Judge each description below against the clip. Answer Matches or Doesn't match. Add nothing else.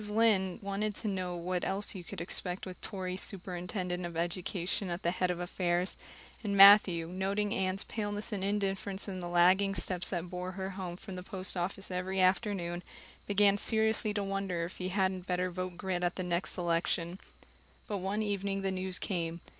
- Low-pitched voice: Doesn't match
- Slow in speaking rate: Doesn't match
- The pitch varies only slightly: Matches